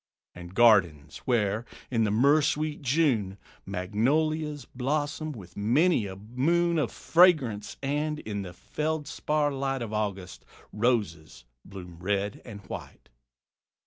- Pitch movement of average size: No, wide, 6.9 semitones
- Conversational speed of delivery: No, slow, 120 wpm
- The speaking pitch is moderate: No, low, 120 Hz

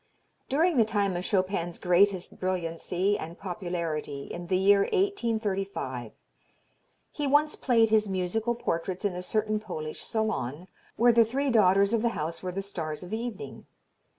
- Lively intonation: No, average, 4.1 semitones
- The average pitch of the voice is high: Yes, high, 195 Hz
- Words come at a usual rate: Yes, average, 155 wpm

